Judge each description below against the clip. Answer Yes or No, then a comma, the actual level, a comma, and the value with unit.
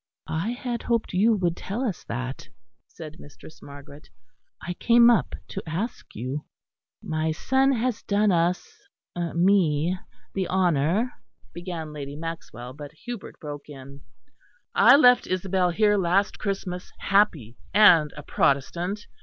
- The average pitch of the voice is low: No, medium, 175 Hz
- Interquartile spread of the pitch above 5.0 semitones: Yes, wide, 5.5 semitones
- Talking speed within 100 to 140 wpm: Yes, slow, 135 wpm